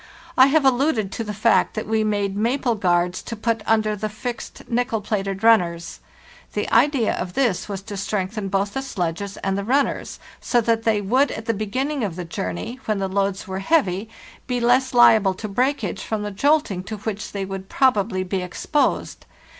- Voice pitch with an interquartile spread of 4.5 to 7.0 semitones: No, average, 3.7 semitones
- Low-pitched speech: No, high, 215 Hz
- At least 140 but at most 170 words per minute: No, average, 190 wpm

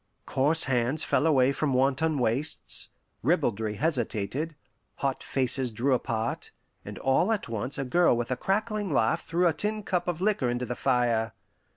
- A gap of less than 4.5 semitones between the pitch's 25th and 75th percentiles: No, average, 5.1 semitones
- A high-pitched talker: No, low, 135 Hz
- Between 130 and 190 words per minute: Yes, average, 165 wpm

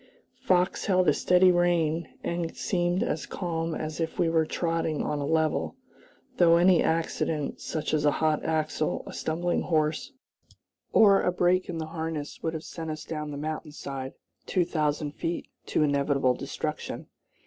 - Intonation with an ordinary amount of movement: No, narrow, 2.3 semitones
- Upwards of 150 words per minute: Yes, average, 165 wpm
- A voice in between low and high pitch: Yes, medium, 160 Hz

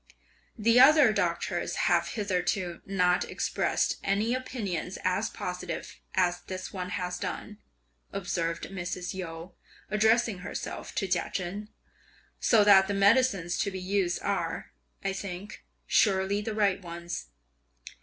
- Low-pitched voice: No, high, 190 Hz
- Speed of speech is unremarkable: No, slow, 125 wpm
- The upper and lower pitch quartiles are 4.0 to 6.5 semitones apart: No, narrow, 2.6 semitones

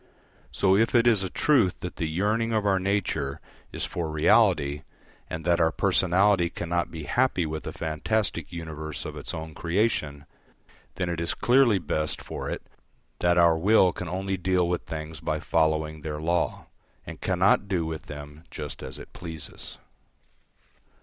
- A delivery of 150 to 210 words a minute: Yes, average, 165 wpm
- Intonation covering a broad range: No, average, 3.6 semitones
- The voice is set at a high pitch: No, very low, 85 Hz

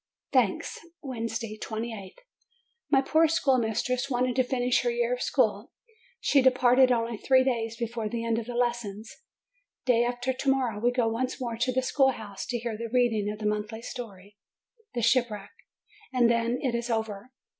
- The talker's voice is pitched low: No, high, 240 Hz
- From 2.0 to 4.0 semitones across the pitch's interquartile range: Yes, narrow, 2.4 semitones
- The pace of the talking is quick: No, average, 170 wpm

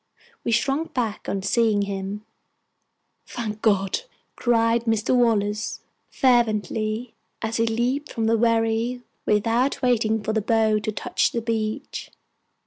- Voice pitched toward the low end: No, high, 225 Hz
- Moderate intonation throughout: No, narrow, 1.8 semitones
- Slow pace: Yes, slow, 130 wpm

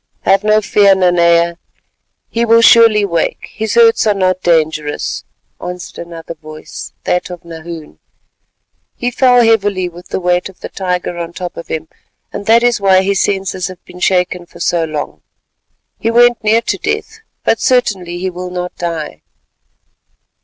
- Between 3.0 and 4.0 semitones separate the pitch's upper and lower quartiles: Yes, average, 3.7 semitones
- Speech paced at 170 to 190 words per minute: No, average, 160 wpm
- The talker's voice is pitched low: No, medium, 185 Hz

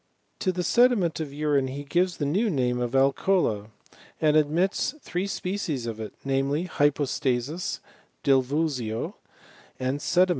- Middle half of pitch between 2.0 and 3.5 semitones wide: No, average, 5.1 semitones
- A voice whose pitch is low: No, medium, 145 Hz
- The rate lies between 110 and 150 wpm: Yes, average, 140 wpm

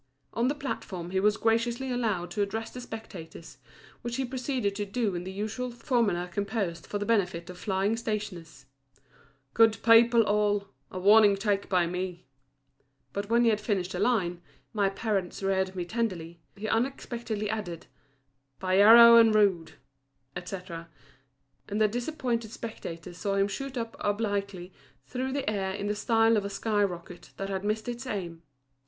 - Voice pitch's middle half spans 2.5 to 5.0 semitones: Yes, average, 3.4 semitones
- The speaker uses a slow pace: No, average, 165 wpm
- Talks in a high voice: Yes, high, 205 Hz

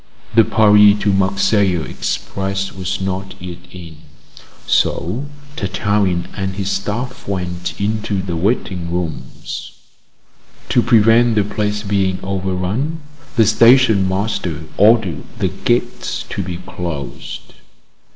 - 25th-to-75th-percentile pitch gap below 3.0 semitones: Yes, narrow, 2.6 semitones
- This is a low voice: Yes, low, 100 Hz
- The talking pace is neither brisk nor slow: No, slow, 110 wpm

